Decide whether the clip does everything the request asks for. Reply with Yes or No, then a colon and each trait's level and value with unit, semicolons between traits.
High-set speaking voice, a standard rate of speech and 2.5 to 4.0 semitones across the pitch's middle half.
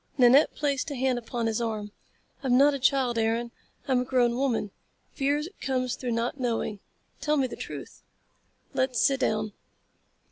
Yes: very high, 250 Hz; average, 165 wpm; average, 2.8 semitones